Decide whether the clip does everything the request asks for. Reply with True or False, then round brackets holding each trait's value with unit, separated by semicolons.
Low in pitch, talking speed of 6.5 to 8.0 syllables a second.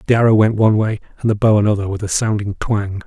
True (105 Hz; 6.8 syllables/s)